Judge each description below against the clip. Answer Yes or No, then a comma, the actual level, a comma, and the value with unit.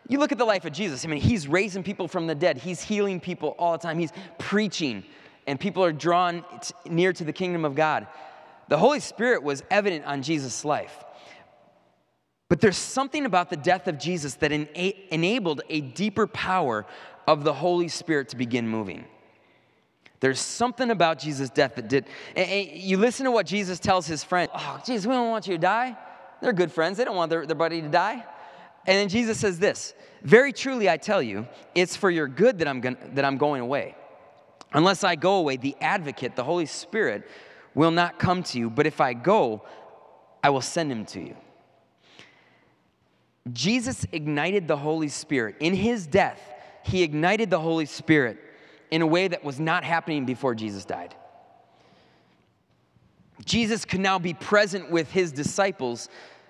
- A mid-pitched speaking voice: Yes, medium, 175 Hz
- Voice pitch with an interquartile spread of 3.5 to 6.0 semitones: Yes, average, 4.4 semitones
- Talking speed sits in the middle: Yes, average, 180 wpm